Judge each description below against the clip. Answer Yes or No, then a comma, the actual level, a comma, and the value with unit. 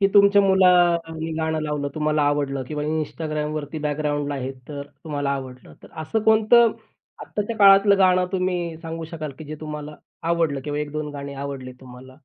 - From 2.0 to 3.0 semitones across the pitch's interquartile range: No, average, 3.7 semitones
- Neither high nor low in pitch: Yes, medium, 155 Hz